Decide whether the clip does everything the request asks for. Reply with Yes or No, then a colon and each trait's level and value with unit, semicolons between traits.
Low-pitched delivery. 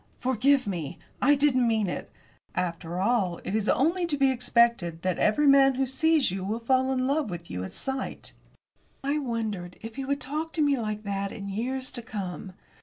No: high, 235 Hz